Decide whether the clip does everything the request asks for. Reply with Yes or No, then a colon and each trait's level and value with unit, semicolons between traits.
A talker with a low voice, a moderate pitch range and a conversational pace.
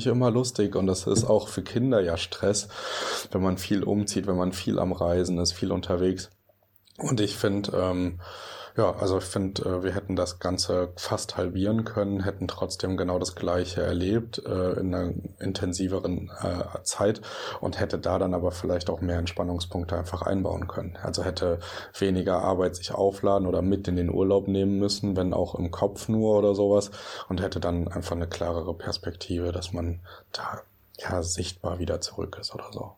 No: very low, 95 Hz; narrow, 2.0 semitones; average, 175 wpm